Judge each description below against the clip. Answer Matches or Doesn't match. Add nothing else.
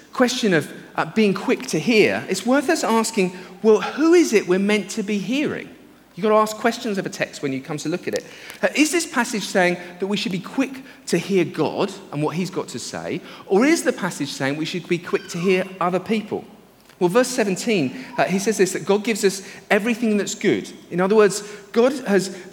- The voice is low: Doesn't match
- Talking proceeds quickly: Matches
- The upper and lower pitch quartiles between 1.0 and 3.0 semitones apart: Doesn't match